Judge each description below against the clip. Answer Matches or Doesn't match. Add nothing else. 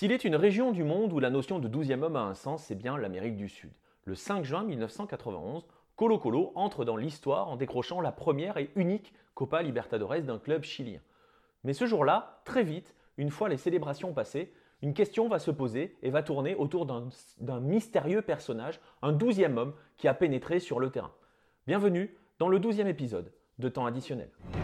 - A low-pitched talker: Doesn't match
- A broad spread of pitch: Matches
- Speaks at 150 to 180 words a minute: Doesn't match